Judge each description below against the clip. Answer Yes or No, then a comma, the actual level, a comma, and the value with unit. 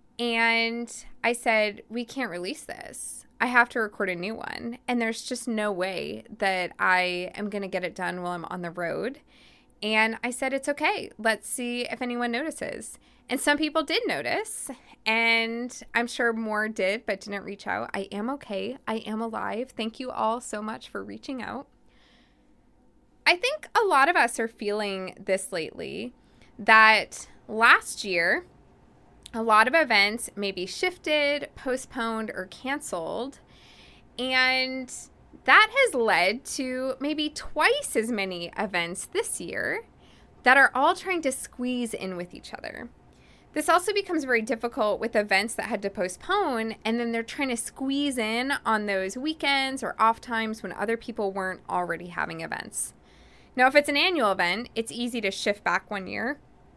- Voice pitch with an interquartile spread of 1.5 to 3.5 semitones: No, average, 3.9 semitones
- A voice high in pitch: Yes, high, 230 Hz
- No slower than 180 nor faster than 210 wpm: No, average, 170 wpm